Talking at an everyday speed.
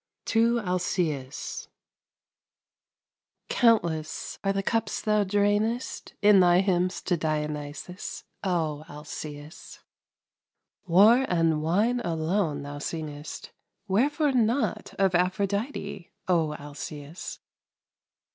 No: slow, 85 wpm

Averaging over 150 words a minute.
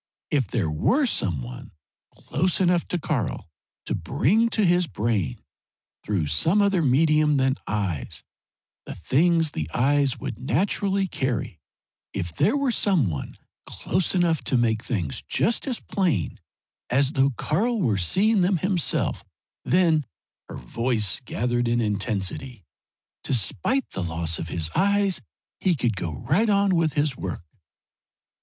No: average, 140 wpm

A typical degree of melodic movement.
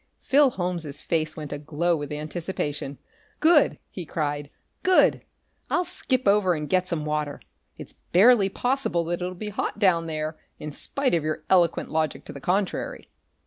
Yes: average, 4.5 semitones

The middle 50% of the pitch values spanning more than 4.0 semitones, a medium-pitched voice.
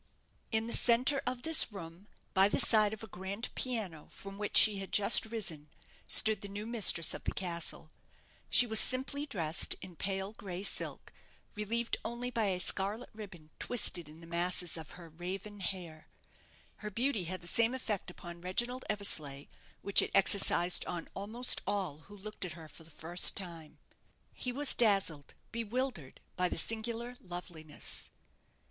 No: average, 4.5 semitones; high, 195 Hz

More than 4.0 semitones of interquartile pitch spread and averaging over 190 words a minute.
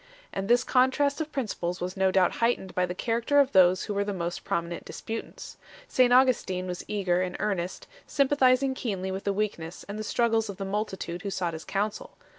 Yes: average, 4.8 semitones; average, 200 wpm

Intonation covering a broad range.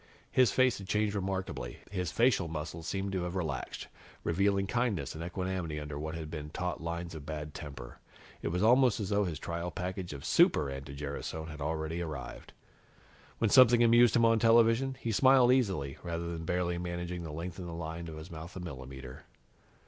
No: average, 4.4 semitones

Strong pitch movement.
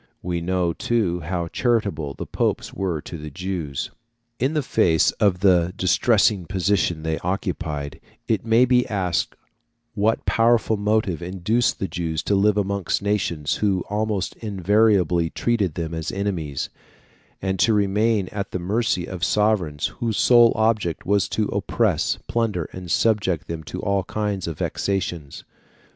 No: average, 3.9 semitones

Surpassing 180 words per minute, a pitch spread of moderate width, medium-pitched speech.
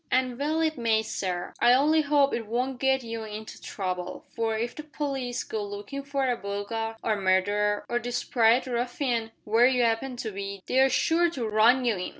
No: average, 190 wpm; average, 3.7 semitones; high, 235 Hz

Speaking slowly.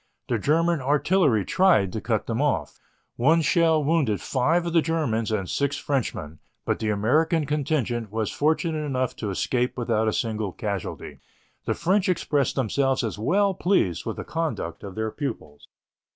No: average, 165 wpm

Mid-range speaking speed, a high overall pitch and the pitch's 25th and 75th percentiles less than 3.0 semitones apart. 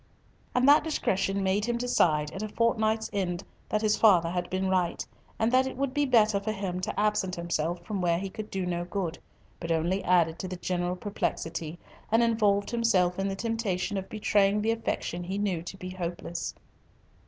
No: average, 195 wpm; high, 195 Hz; average, 3.5 semitones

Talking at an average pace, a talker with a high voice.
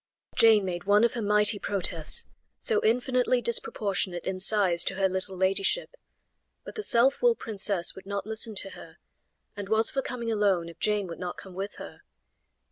Yes: average, 180 wpm; high, 205 Hz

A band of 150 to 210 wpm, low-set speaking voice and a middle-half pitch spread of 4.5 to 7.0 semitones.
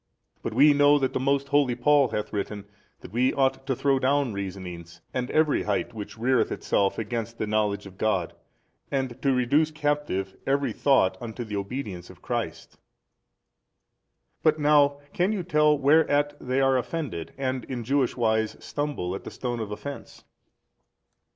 Yes: average, 165 wpm; low, 130 Hz; average, 5.0 semitones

